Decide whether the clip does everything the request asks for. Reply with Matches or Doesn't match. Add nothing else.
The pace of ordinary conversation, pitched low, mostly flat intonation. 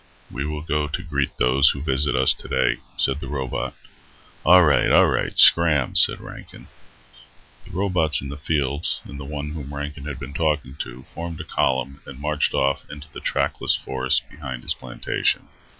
Matches